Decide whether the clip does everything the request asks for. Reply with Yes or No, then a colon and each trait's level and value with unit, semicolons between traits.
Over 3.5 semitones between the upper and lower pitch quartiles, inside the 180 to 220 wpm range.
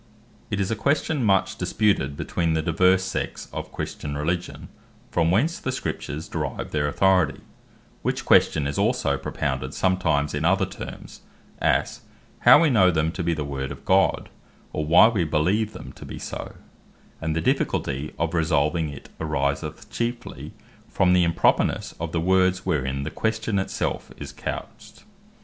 No: average, 4.1 semitones; average, 165 wpm